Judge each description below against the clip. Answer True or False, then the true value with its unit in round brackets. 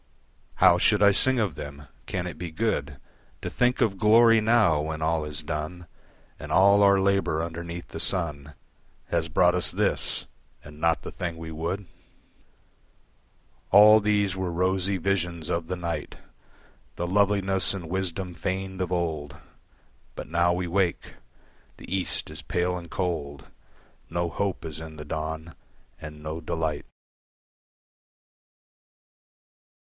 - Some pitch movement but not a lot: True (3.2 semitones)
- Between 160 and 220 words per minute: False (140 wpm)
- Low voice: True (85 Hz)